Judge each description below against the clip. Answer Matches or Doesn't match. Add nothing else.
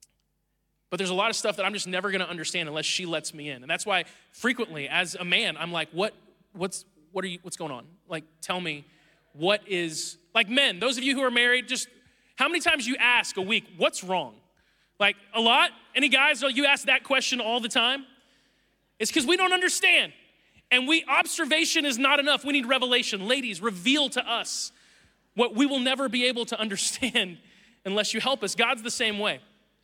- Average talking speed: Doesn't match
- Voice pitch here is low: Doesn't match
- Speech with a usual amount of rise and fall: Doesn't match